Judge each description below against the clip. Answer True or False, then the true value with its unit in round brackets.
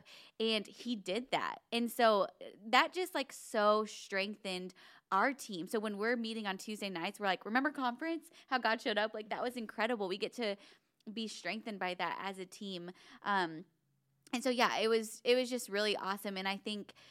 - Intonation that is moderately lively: True (3.6 semitones)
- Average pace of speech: True (195 wpm)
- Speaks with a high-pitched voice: True (215 Hz)